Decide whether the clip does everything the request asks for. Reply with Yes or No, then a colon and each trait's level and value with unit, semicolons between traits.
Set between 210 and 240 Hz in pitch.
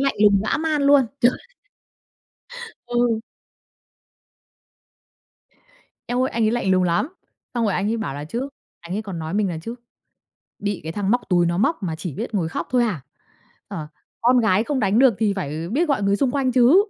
Yes: high, 215 Hz